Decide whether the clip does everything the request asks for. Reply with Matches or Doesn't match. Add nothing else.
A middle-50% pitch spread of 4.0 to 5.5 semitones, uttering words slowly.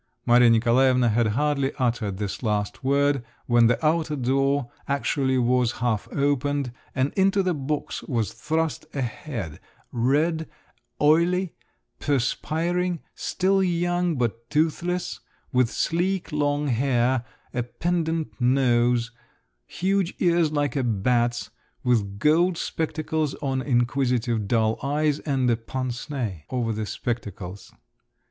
Matches